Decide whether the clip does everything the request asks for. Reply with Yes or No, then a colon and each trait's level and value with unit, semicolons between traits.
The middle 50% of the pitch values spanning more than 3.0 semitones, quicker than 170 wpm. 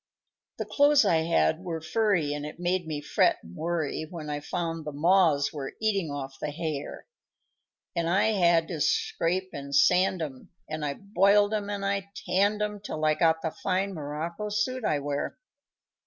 Yes: average, 4.7 semitones; average, 185 wpm